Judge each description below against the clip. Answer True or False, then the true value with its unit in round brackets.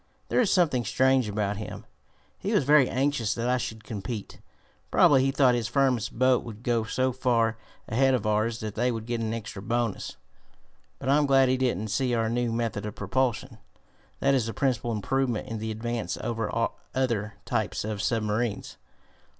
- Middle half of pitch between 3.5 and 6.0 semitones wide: False (2.9 semitones)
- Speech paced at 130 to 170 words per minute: False (180 wpm)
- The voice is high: False (120 Hz)